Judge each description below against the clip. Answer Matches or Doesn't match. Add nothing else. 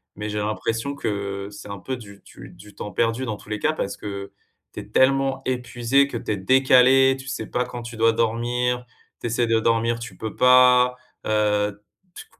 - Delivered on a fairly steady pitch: Doesn't match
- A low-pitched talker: Matches